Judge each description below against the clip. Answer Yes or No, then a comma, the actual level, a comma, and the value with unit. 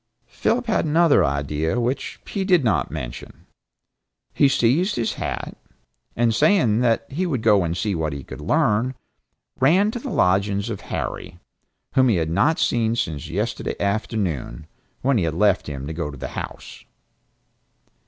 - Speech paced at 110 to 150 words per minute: No, average, 160 wpm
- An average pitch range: No, wide, 8.8 semitones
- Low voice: Yes, low, 110 Hz